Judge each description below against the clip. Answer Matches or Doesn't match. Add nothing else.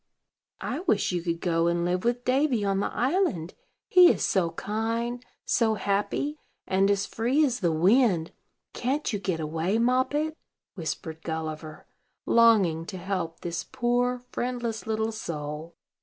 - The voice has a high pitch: Matches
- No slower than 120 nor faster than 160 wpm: Matches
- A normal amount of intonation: Doesn't match